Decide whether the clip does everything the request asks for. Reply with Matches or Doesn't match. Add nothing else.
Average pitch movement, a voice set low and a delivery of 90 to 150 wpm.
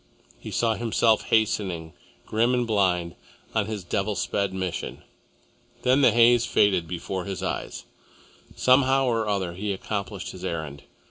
Matches